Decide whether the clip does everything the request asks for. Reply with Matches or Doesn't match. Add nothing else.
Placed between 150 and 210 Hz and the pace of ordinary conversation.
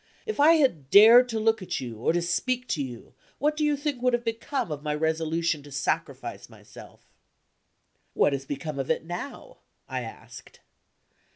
Matches